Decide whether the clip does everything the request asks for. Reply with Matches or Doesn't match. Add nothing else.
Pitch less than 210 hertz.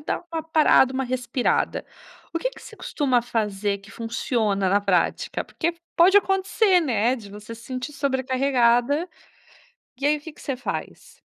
Doesn't match